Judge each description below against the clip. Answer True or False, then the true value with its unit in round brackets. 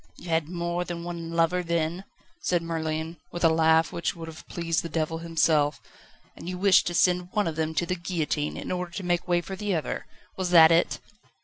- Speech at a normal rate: False (215 wpm)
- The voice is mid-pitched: True (170 Hz)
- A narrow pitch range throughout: True (1.6 semitones)